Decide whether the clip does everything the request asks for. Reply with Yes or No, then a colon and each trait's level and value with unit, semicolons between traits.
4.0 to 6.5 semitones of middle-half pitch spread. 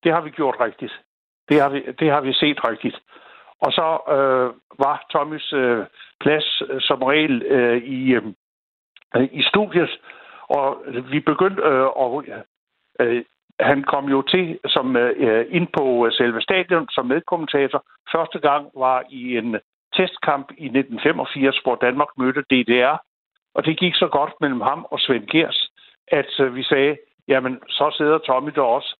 No: average, 3.2 semitones